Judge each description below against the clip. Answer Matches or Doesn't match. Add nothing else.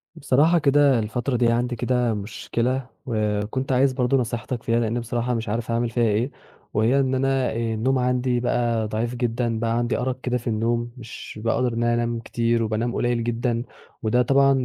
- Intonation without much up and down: Matches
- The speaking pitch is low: Matches